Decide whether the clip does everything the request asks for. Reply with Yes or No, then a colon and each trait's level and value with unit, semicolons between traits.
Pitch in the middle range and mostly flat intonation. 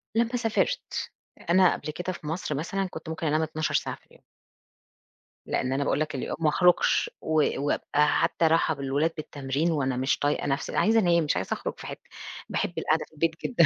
No: medium, 160 Hz; average, 3.2 semitones